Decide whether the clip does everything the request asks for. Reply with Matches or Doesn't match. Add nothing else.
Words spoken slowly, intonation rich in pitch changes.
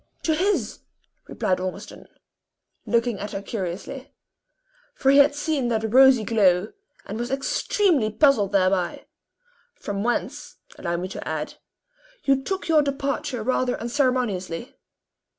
Matches